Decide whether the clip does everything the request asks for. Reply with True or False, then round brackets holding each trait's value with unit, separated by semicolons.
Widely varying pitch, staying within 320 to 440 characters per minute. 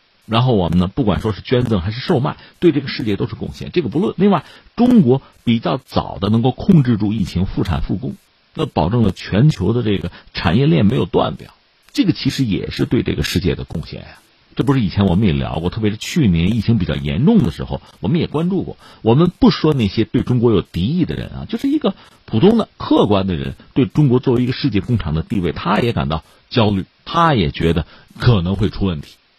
True (5.8 semitones; 335 characters per minute)